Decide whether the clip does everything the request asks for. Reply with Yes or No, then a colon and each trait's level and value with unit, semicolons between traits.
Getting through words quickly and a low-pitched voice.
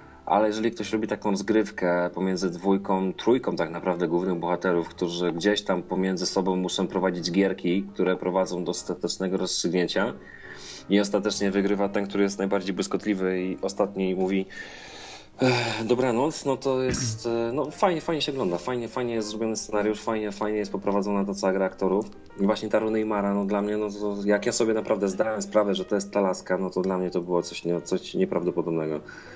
Yes: fast, 185 wpm; low, 100 Hz